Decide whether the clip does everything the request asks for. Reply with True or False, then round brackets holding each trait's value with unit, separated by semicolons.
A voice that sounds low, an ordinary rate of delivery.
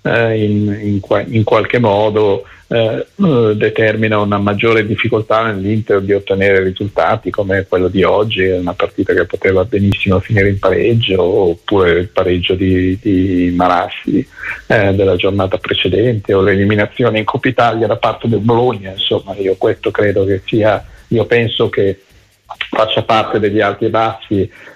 True (105 Hz; 150 wpm)